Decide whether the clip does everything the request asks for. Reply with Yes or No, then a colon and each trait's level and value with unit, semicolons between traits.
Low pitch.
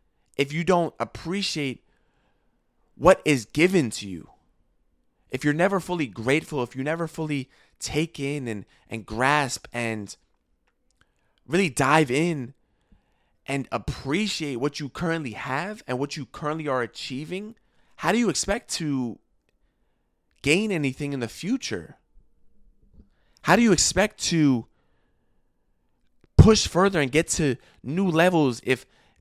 No: medium, 145 Hz